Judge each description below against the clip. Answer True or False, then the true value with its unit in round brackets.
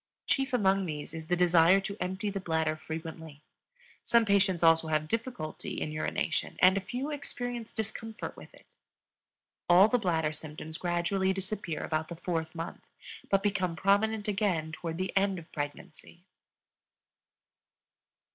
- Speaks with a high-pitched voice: False (180 Hz)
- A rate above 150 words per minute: False (145 wpm)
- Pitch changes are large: False (3.9 semitones)